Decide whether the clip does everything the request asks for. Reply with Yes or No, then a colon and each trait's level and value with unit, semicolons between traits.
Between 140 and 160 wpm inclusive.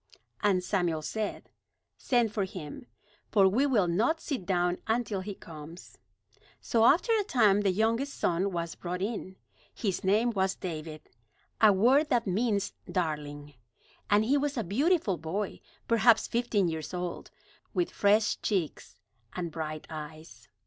Yes: average, 145 wpm